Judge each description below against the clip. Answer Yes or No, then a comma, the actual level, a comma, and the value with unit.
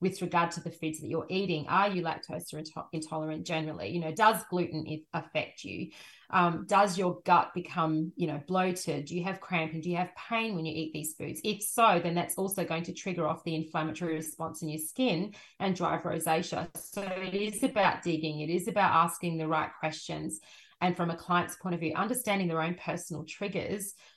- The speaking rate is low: No, fast, 205 wpm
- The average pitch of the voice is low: No, medium, 170 Hz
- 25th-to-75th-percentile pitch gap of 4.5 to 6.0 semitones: No, average, 2.8 semitones